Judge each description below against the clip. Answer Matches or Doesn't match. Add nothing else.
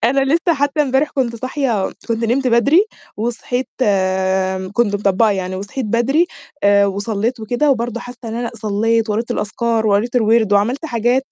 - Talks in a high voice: Matches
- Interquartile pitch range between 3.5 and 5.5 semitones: Matches